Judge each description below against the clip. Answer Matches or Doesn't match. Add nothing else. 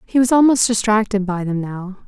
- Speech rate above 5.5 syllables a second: Doesn't match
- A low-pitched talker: Doesn't match